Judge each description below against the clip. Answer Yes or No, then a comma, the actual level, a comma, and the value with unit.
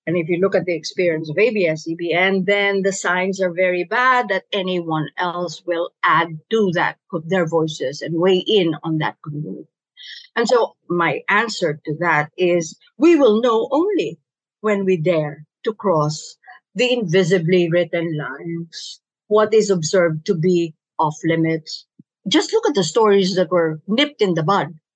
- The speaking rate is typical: No, fast, 170 wpm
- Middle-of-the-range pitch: Yes, medium, 180 Hz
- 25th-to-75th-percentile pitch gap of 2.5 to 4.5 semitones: Yes, average, 3.5 semitones